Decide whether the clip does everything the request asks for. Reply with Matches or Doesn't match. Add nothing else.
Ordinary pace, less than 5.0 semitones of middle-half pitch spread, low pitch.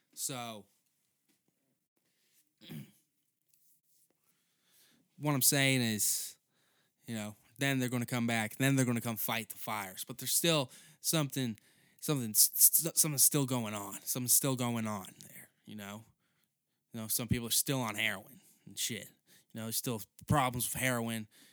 Matches